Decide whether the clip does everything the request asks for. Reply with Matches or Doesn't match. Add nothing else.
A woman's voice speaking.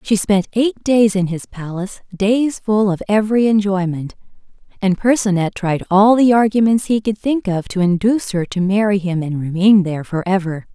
Matches